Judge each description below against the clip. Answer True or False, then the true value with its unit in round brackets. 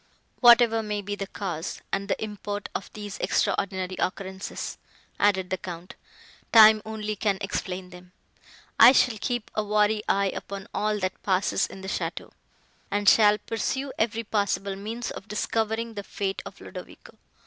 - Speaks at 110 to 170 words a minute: True (155 wpm)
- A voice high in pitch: True (205 Hz)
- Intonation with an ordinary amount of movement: False (2.2 semitones)